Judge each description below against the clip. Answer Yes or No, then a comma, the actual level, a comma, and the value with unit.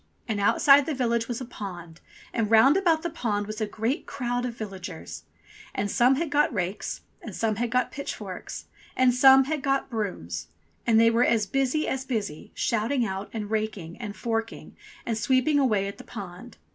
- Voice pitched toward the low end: No, high, 230 Hz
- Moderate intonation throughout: Yes, average, 4.2 semitones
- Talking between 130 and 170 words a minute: No, average, 185 wpm